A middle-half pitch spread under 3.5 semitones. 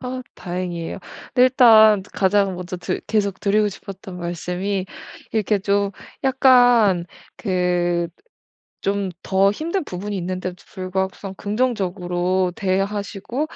Yes: average, 2.7 semitones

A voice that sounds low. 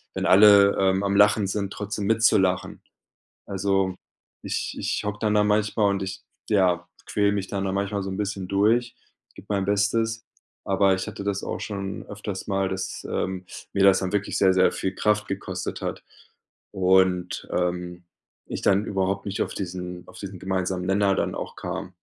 Yes: low, 100 Hz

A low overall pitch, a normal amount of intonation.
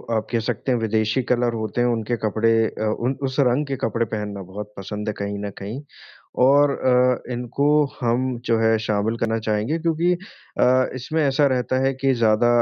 Yes: low, 120 Hz; average, 3.1 semitones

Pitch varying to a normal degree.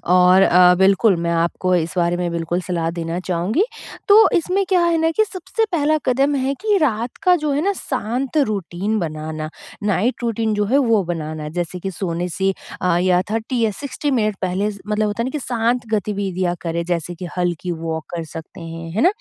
No: wide, 6.4 semitones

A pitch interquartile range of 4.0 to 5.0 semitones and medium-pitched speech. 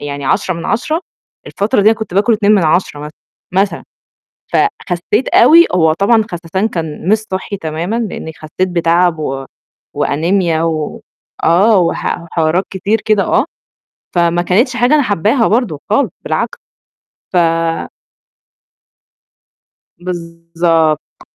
Yes: average, 4.5 semitones; medium, 180 Hz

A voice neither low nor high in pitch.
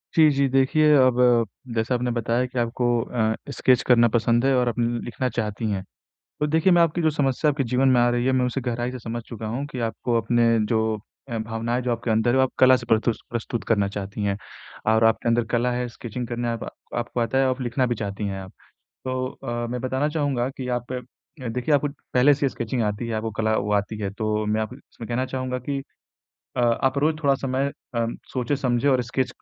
No: low, 120 Hz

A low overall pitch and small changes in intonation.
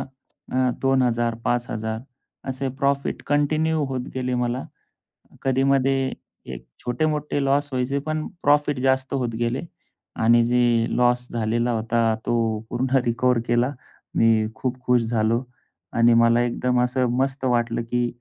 Yes: low, 125 Hz; narrow, 2.3 semitones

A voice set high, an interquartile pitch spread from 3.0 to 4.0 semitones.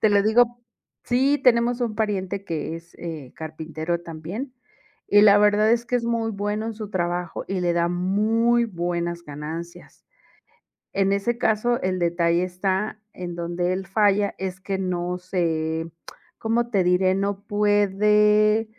Yes: high, 195 Hz; average, 3.7 semitones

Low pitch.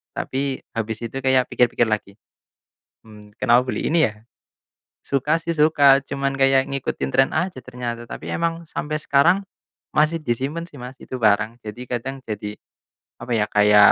Yes: low, 130 Hz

